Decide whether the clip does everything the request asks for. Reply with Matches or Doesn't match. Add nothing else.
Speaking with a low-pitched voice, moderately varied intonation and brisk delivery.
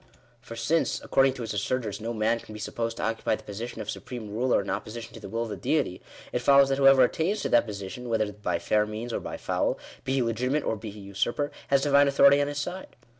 Matches